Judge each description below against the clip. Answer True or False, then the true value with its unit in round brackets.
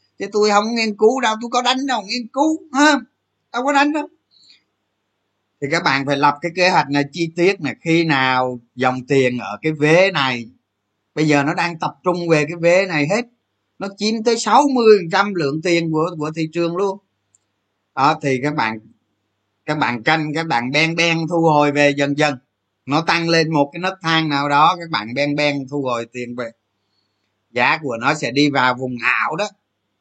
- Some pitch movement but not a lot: False (6.5 semitones)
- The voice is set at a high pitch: False (150 Hz)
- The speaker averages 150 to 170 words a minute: False (200 wpm)